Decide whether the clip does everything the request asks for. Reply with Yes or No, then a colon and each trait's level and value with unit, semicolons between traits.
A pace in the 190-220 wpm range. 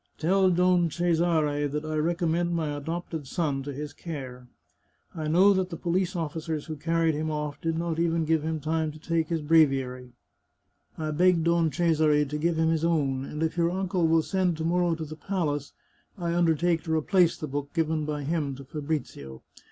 Yes: average, 195 wpm